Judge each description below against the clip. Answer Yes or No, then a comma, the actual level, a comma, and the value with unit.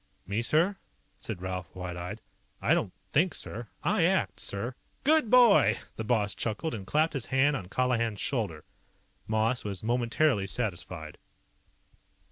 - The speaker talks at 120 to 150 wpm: Yes, average, 140 wpm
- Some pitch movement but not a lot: No, wide, 5.7 semitones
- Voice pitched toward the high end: No, low, 115 Hz